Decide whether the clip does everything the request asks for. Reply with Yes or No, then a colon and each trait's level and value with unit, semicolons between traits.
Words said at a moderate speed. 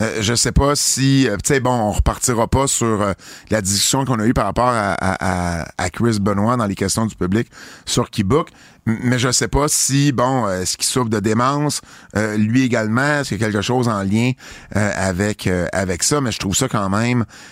No: fast, 225 wpm